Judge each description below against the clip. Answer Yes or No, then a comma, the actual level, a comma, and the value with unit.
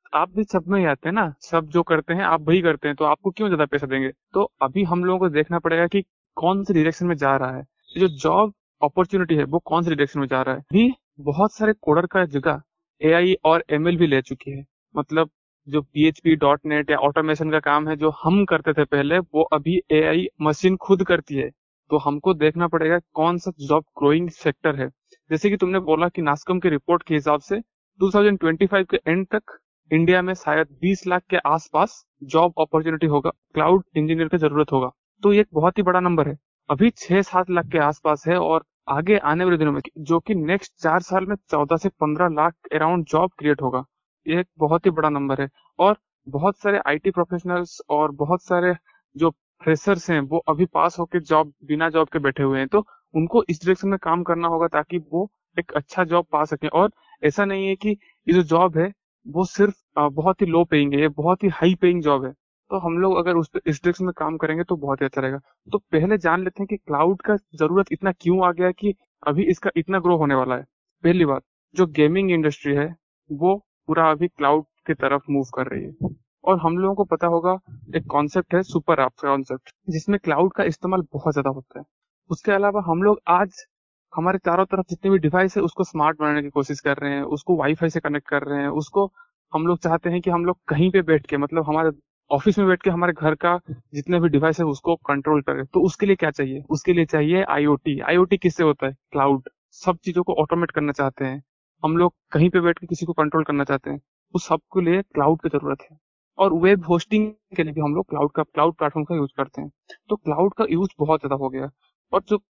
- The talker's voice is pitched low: No, medium, 165 Hz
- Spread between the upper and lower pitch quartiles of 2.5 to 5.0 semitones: Yes, average, 3.5 semitones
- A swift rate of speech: Yes, fast, 205 wpm